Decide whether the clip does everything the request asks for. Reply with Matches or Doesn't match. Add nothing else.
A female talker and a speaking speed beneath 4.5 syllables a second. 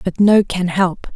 Matches